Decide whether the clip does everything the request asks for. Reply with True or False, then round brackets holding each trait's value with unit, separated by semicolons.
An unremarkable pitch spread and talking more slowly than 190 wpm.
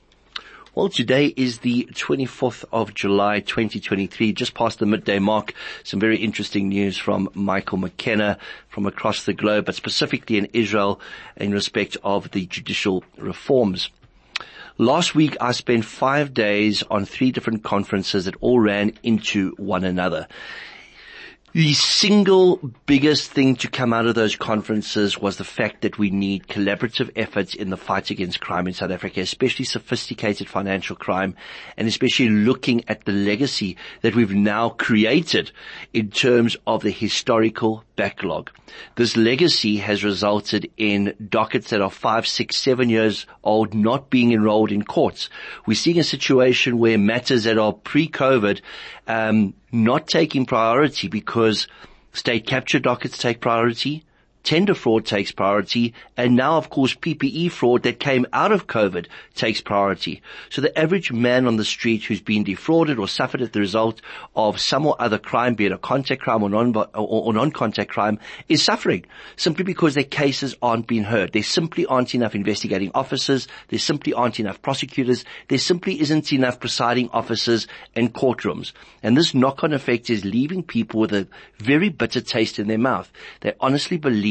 True (3.9 semitones; 160 wpm)